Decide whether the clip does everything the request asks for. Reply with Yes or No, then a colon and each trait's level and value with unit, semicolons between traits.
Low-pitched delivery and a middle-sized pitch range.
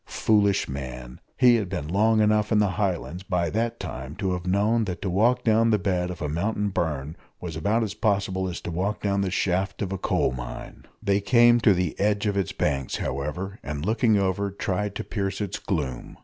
Yes: very low, 95 Hz; average, 3.4 semitones